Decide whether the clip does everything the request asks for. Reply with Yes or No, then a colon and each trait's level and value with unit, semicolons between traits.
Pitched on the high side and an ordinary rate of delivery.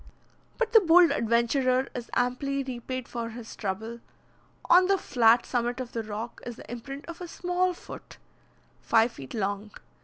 Yes: high, 245 Hz; average, 160 wpm